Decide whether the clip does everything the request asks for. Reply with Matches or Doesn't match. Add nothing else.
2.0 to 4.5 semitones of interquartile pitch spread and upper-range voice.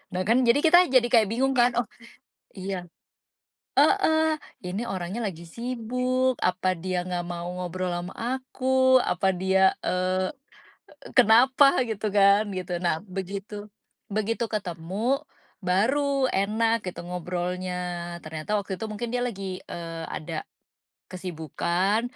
Doesn't match